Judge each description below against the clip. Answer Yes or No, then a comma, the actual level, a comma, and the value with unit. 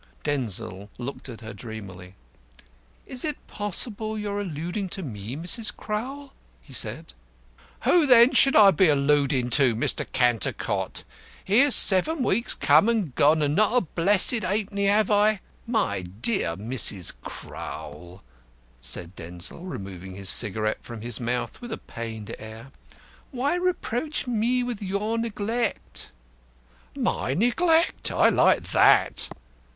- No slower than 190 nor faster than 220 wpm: No, slow, 135 wpm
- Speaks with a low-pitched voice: No, medium, 175 Hz